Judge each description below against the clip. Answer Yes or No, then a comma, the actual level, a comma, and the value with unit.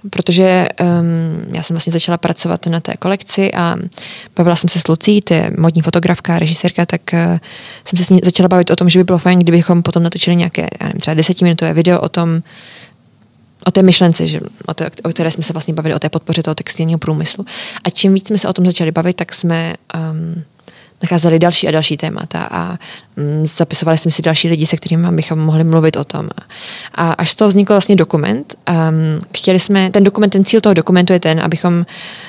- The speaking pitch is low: No, medium, 170 Hz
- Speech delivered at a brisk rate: Yes, fast, 210 wpm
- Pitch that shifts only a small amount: Yes, narrow, 1.9 semitones